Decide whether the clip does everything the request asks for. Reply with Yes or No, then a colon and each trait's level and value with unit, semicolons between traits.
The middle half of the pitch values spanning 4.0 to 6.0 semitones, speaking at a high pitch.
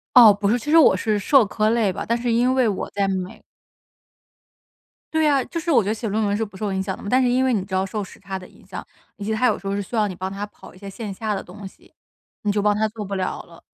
No: average, 3.0 semitones; high, 210 Hz